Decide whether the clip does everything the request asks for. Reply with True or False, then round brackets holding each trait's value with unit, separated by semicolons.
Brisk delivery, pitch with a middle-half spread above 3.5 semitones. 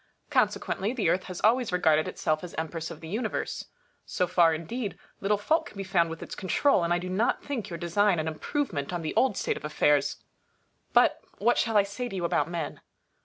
True (215 wpm; 4.4 semitones)